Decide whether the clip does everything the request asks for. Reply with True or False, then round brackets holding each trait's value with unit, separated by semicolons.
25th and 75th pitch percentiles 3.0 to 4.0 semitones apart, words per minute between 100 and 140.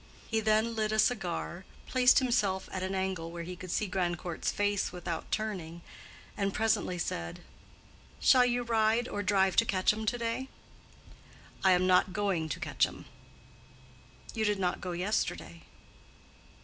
False (3.4 semitones; 150 wpm)